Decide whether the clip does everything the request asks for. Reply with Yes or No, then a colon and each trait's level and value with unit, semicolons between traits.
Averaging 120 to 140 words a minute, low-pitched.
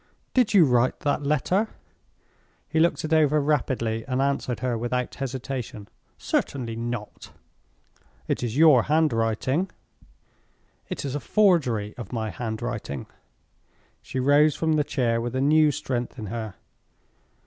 Yes: slow, 135 wpm; low, 130 Hz